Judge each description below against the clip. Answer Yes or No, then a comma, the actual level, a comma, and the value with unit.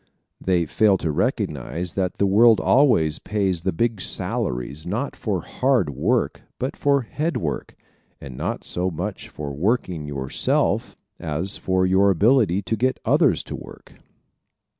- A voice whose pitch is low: Yes, very low, 95 Hz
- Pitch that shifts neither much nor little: No, wide, 6.0 semitones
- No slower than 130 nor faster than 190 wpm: Yes, average, 145 wpm